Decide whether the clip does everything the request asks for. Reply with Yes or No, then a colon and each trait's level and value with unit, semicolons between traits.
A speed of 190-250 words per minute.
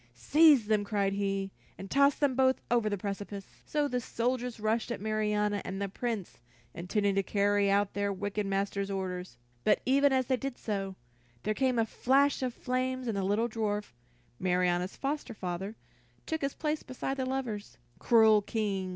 No: average, 175 wpm